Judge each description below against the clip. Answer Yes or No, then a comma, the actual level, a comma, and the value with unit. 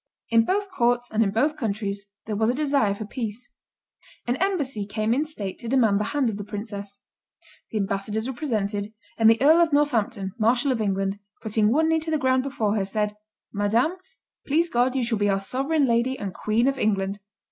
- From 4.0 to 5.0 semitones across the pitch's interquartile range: Yes, average, 4.7 semitones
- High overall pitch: Yes, high, 225 Hz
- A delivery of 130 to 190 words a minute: No, average, 200 wpm